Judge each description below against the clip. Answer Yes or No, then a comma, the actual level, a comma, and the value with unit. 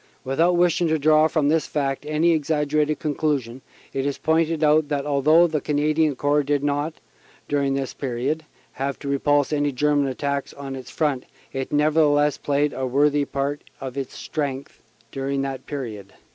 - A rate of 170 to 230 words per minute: Yes, average, 175 wpm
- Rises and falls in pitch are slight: Yes, narrow, 1.9 semitones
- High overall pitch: No, medium, 145 Hz